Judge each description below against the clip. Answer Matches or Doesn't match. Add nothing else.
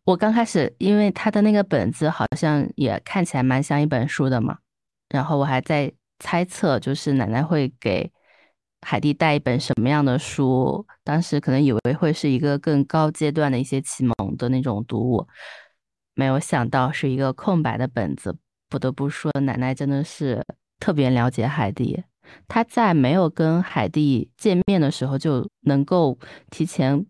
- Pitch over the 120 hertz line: Matches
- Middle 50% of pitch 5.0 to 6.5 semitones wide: Doesn't match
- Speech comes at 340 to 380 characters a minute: Doesn't match